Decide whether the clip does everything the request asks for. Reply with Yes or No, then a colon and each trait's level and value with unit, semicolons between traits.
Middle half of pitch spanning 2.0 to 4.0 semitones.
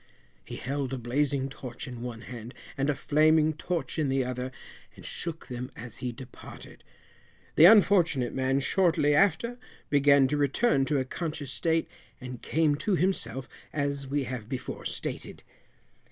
Yes: average, 3.5 semitones